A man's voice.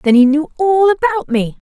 No: female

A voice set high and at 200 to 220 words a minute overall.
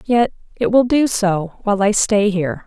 Yes: high, 210 Hz; fast, 205 wpm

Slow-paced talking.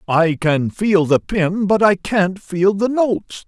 No: average, 190 wpm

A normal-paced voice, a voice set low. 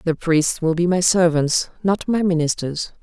No: average, 180 wpm; medium, 170 Hz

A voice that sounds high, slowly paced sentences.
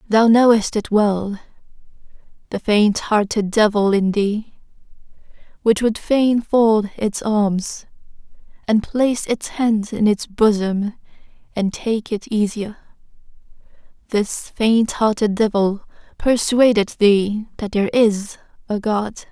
Yes: high, 215 Hz; slow, 115 wpm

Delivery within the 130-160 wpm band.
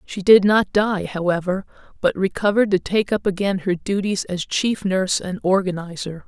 No: average, 170 wpm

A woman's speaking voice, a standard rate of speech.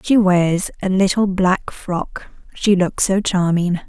Yes: female; average, 155 wpm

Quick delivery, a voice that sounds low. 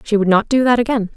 No: fast, 310 wpm; high, 220 Hz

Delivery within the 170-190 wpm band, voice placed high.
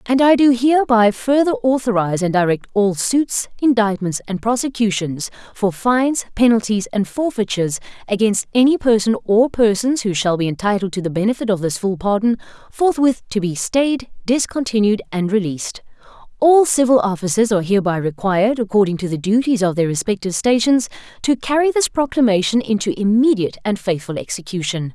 No: average, 155 wpm; high, 215 Hz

